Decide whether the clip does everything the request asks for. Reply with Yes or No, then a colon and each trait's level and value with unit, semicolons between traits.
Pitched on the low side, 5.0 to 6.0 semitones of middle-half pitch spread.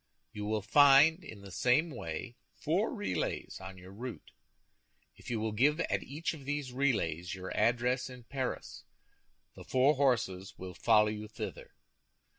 Yes: low, 120 Hz; wide, 5.6 semitones